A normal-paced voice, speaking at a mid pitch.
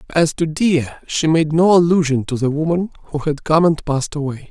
No: fast, 215 wpm; medium, 155 Hz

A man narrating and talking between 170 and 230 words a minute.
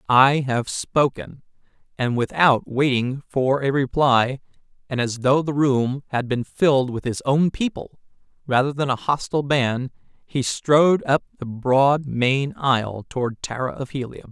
No: male; average, 155 wpm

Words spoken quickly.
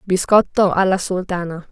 No: slow, 105 wpm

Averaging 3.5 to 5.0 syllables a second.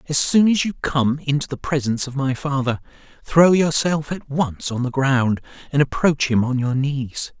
Yes: 4.6 syllables/s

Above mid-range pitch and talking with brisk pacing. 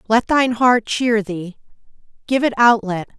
No: high, 225 Hz; average, 170 wpm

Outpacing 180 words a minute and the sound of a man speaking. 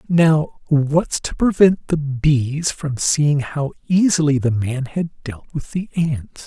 No: average, 160 wpm; male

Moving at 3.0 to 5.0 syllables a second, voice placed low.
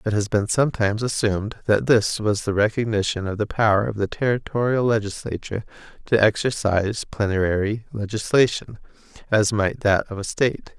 No: 5.4 syllables/s; low, 105 Hz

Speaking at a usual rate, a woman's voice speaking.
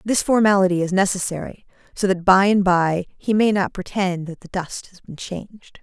Yes: average, 195 wpm; female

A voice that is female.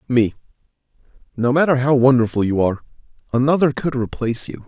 No: male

